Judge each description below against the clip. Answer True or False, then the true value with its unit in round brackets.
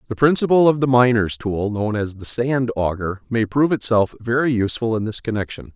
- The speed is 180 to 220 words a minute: True (200 wpm)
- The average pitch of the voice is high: False (115 Hz)